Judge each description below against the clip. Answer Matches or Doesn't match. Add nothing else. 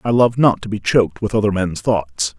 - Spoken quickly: Matches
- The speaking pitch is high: Doesn't match